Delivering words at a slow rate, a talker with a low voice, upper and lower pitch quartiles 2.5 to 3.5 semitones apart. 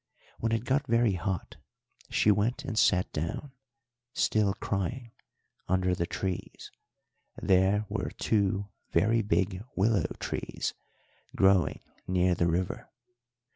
Yes: slow, 115 wpm; low, 100 Hz; average, 3.2 semitones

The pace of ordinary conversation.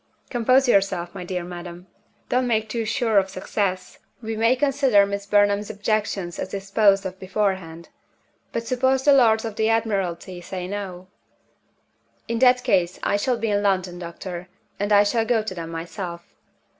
Yes: average, 165 wpm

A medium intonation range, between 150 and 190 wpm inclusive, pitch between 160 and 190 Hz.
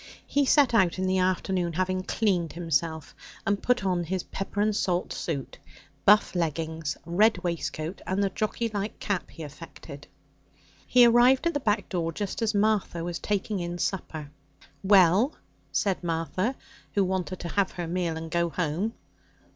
Yes: average, 3.5 semitones; average, 165 wpm; medium, 185 Hz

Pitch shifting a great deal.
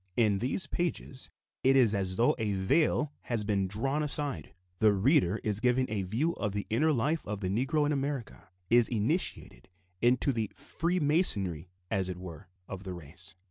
Yes: wide, 6.4 semitones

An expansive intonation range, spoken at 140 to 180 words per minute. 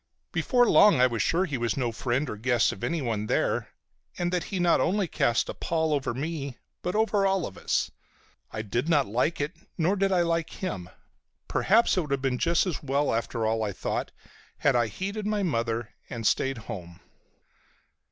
No: wide, 7.2 semitones; average, 195 wpm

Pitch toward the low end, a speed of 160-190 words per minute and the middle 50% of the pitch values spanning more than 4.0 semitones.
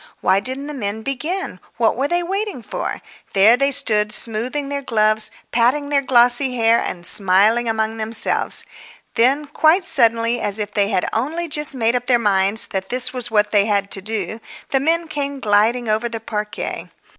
No: high, 235 Hz; average, 180 wpm; average, 4.5 semitones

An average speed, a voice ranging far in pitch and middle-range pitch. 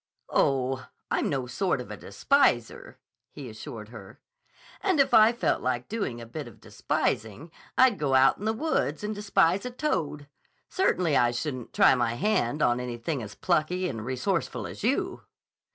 Yes: average, 170 wpm; wide, 8.9 semitones; medium, 150 Hz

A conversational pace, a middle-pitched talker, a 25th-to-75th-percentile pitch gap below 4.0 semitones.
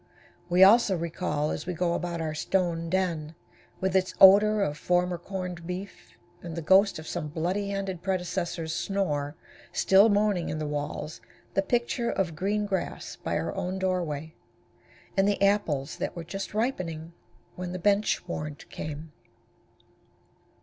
Yes: average, 150 wpm; medium, 180 Hz; average, 3.3 semitones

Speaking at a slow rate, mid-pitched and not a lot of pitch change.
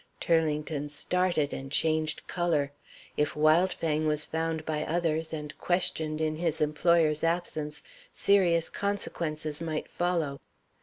Yes: slow, 115 wpm; medium, 155 Hz; narrow, 2.0 semitones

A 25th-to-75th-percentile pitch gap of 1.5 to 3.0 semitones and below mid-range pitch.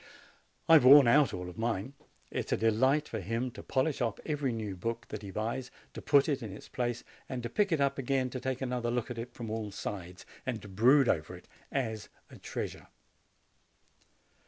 No: average, 3.5 semitones; low, 120 Hz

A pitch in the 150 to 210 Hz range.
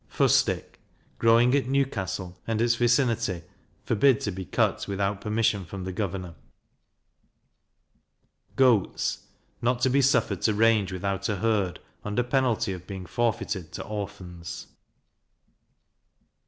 No: low, 105 Hz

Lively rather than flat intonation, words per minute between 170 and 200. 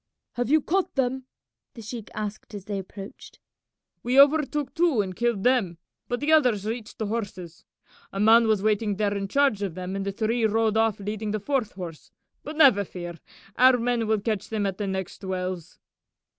No: average, 3.8 semitones; average, 190 wpm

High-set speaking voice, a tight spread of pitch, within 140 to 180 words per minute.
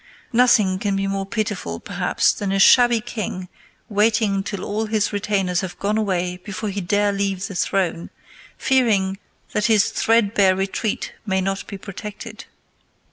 Yes: high, 200 Hz; narrow, 2.0 semitones; average, 150 wpm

